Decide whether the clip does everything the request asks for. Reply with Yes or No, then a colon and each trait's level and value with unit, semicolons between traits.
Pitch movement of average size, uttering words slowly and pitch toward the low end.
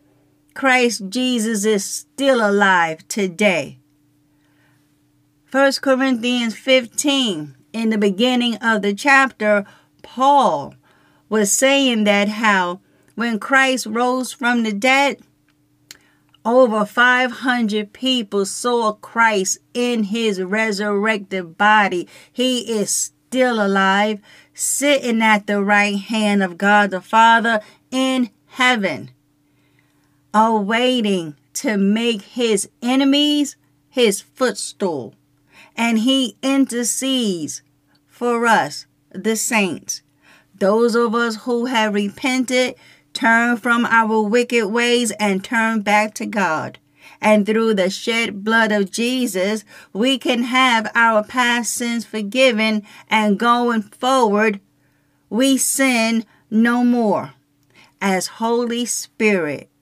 No: average, 3.5 semitones; slow, 105 wpm; high, 220 Hz